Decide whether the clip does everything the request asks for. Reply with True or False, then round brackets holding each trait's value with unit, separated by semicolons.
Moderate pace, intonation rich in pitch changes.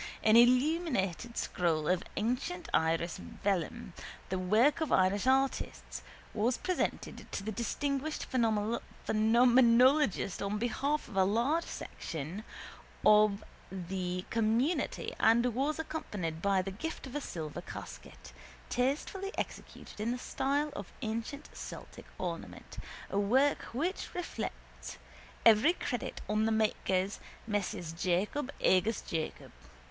False (120 wpm; 5.8 semitones)